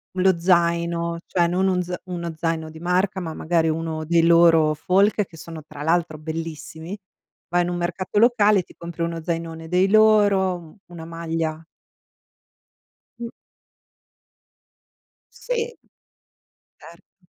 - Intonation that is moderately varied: No, narrow, 2.2 semitones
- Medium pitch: Yes, medium, 170 Hz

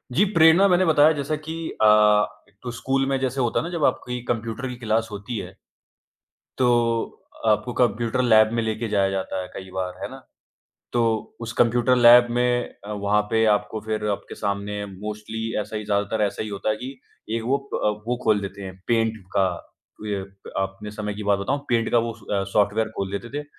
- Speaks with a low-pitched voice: Yes, low, 110 Hz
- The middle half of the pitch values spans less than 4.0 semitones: Yes, average, 3.1 semitones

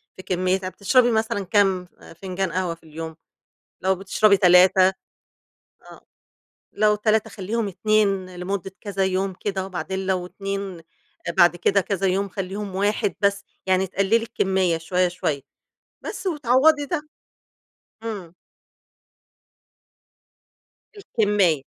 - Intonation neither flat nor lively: No, narrow, 2.2 semitones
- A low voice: No, high, 195 Hz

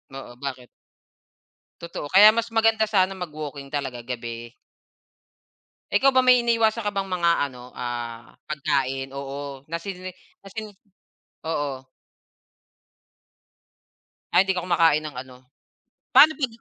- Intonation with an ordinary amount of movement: No, wide, 7.5 semitones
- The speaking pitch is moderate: Yes, medium, 155 Hz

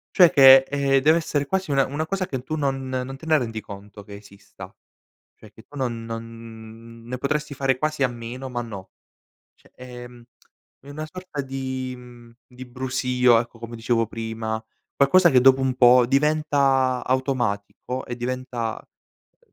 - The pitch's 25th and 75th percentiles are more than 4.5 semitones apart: No, average, 2.8 semitones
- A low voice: Yes, low, 130 Hz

